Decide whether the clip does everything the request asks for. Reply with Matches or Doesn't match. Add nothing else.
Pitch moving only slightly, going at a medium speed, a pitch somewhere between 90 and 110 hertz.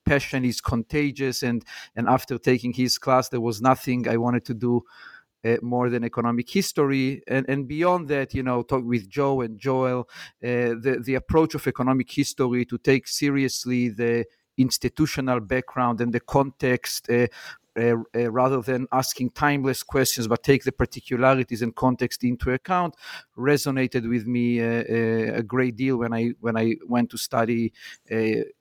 Doesn't match